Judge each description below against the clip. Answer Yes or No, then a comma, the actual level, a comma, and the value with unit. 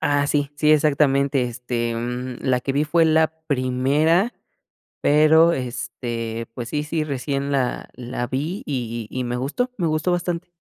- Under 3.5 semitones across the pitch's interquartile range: No, average, 3.8 semitones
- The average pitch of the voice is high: No, medium, 140 Hz